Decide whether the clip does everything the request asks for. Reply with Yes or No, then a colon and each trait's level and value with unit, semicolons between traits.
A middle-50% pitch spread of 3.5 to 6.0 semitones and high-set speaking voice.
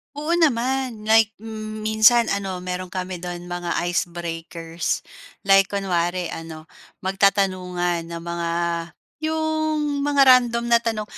Yes: average, 5.2 semitones; high, 195 Hz